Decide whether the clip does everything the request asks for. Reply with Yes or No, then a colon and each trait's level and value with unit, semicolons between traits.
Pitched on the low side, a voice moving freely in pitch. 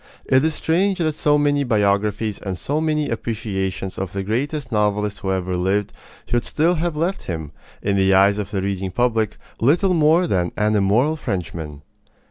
Yes: low, 105 Hz; wide, 7.3 semitones